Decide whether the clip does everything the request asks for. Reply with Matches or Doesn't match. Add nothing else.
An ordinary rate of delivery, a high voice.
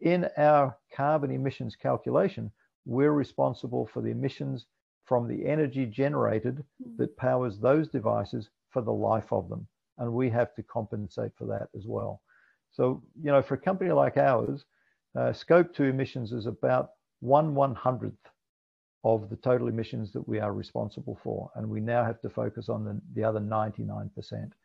Doesn't match